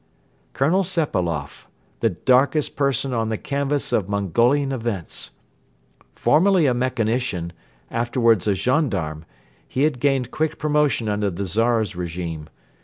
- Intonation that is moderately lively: No, wide, 6.0 semitones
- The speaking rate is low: Yes, slow, 120 wpm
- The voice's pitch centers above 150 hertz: No, low, 120 Hz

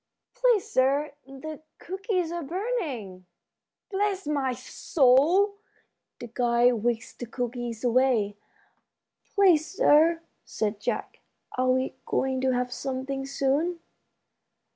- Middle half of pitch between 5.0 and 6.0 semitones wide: Yes, wide, 5.6 semitones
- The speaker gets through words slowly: Yes, slow, 105 wpm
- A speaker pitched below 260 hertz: No, very high, 270 Hz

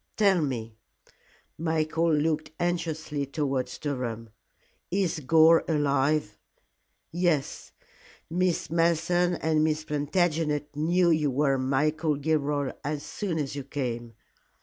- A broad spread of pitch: No, average, 2.8 semitones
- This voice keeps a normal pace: No, slow, 105 wpm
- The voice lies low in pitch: No, medium, 155 Hz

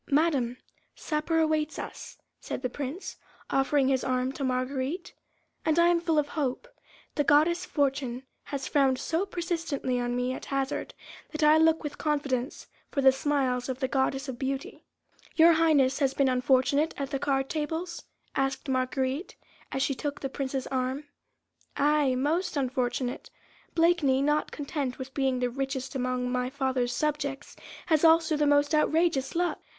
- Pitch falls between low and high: No, very high, 275 Hz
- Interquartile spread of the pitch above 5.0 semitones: No, average, 2.9 semitones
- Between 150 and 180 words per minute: Yes, average, 160 wpm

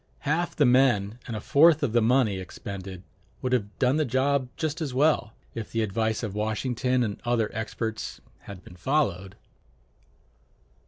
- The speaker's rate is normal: Yes, average, 160 wpm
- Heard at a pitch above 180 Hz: No, low, 120 Hz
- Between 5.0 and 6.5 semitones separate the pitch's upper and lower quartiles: No, average, 4.3 semitones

